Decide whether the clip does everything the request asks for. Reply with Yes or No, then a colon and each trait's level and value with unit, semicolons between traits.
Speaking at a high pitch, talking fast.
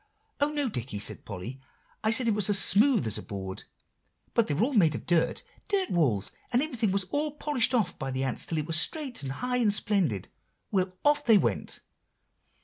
Yes: high, 200 Hz; fast, 210 wpm